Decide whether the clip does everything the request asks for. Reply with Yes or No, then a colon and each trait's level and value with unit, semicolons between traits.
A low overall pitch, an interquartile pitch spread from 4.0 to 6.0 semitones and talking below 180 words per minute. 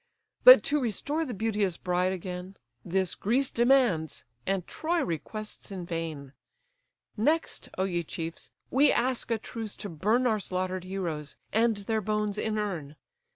No: high, 200 Hz; average, 4.4 semitones; average, 145 wpm